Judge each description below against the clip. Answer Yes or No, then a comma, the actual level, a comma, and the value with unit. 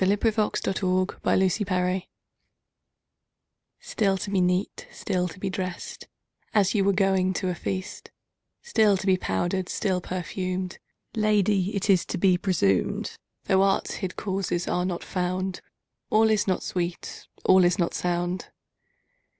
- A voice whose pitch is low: No, medium, 185 Hz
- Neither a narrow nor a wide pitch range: No, narrow, 1.5 semitones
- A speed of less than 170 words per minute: Yes, average, 140 wpm